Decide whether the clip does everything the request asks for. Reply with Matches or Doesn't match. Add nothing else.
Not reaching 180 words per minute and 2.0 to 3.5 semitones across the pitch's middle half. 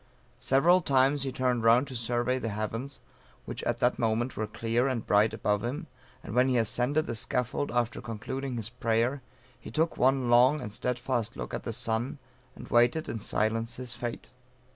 Doesn't match